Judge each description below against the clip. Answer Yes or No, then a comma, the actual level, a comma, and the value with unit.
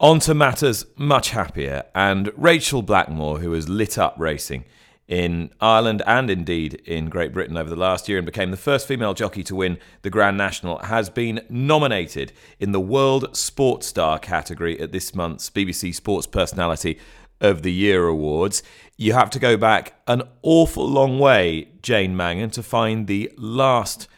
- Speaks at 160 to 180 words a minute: Yes, average, 170 wpm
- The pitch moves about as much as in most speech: No, wide, 5.7 semitones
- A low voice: Yes, low, 100 Hz